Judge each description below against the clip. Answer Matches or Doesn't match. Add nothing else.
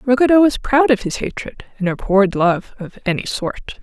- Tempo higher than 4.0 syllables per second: Matches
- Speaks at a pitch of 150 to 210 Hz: Doesn't match